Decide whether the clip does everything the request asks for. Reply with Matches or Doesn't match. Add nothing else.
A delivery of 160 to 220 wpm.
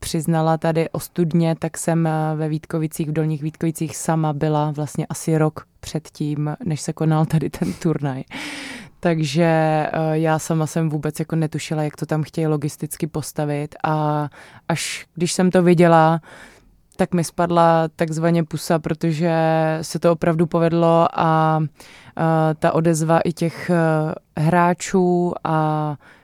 Doesn't match